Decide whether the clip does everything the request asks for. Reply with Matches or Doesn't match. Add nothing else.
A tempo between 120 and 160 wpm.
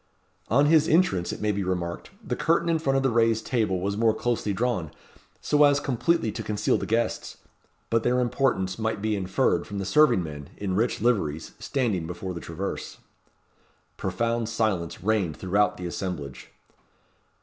Doesn't match